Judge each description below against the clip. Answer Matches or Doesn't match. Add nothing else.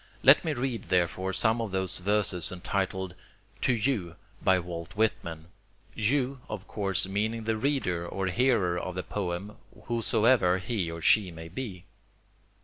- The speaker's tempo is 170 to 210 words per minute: Doesn't match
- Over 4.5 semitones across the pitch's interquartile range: Doesn't match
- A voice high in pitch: Doesn't match